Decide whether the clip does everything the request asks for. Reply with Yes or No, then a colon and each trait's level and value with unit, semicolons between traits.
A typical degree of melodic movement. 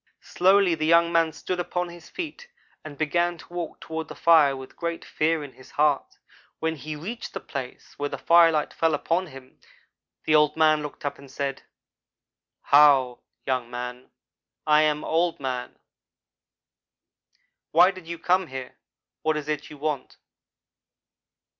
Yes: average, 3.0 semitones